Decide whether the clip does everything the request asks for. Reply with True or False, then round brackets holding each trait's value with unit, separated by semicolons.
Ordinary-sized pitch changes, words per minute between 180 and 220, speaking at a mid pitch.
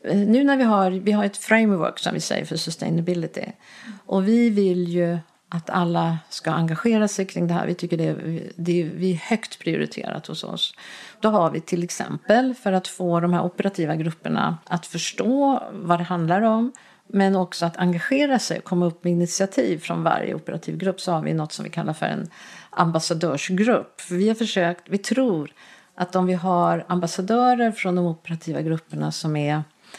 True (3.7 semitones; 190 wpm; 180 Hz)